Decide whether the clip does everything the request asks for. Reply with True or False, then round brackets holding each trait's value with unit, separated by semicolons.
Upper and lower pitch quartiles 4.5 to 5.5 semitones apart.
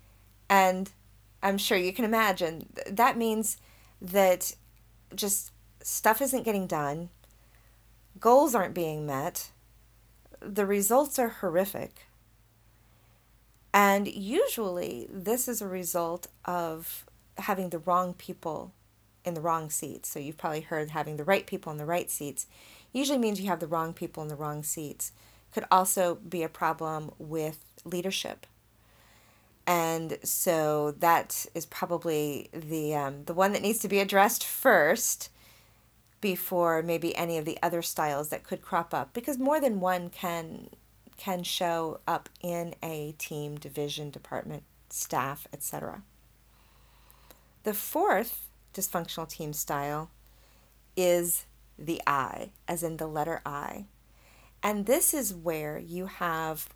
True (4.8 semitones)